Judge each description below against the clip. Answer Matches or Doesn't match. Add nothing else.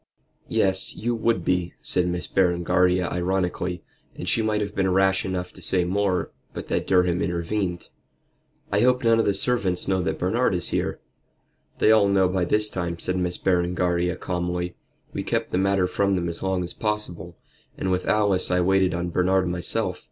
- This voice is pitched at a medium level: Doesn't match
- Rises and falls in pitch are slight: Matches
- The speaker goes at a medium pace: Matches